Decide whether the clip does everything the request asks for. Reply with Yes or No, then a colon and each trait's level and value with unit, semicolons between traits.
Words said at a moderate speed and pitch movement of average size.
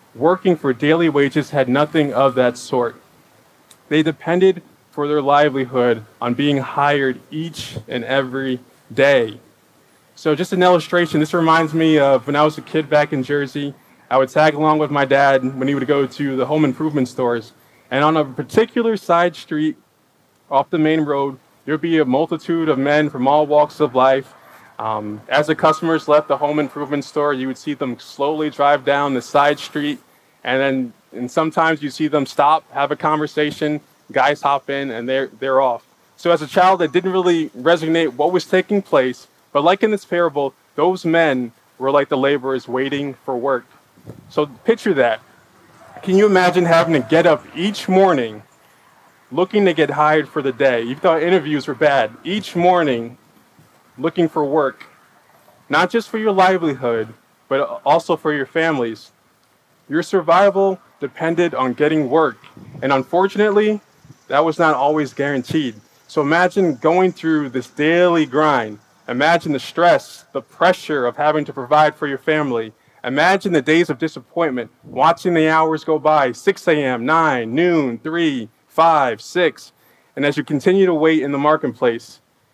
Yes: average, 170 wpm; average, 3.4 semitones